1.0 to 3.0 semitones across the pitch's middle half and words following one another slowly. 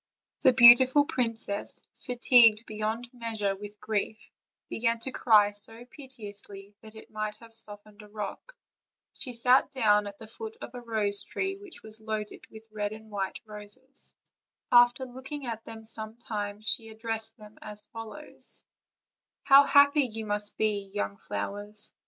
No: average, 2.7 semitones; average, 160 wpm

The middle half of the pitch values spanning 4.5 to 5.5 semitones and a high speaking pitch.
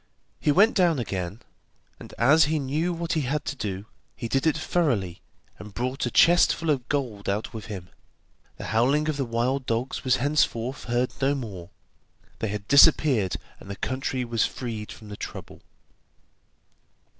No: average, 5.1 semitones; low, 125 Hz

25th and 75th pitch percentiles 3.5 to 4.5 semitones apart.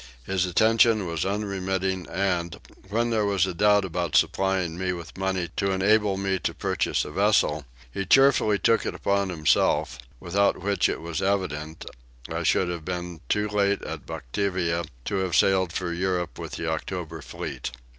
No: narrow, 2.6 semitones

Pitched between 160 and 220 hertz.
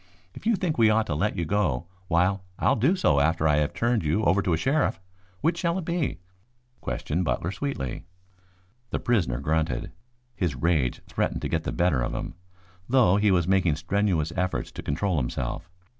No: very low, 90 Hz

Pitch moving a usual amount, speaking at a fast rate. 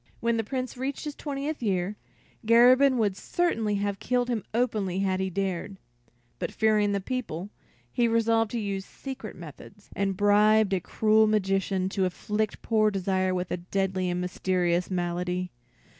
No: average, 3.4 semitones; average, 160 wpm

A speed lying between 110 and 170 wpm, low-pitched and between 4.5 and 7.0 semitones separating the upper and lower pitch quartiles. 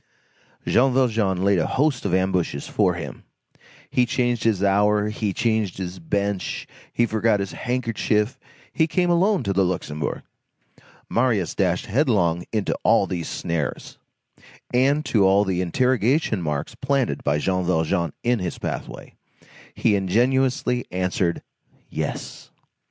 Yes: slow, 135 wpm; low, 105 Hz; average, 5.1 semitones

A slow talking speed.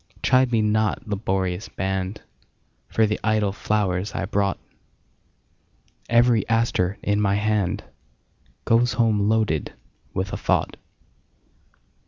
Yes: slow, 95 wpm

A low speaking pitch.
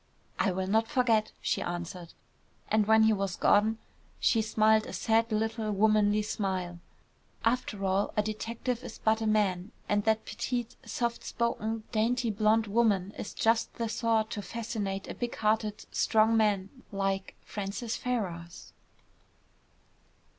No: high, 215 Hz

